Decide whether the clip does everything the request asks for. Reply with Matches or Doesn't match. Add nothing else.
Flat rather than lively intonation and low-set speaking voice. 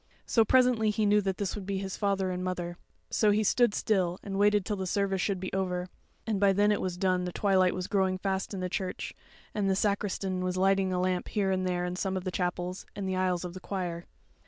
Doesn't match